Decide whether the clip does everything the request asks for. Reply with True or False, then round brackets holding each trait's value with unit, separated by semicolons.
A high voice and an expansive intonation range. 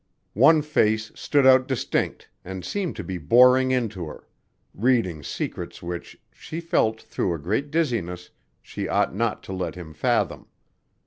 False (110 Hz; 6.5 semitones)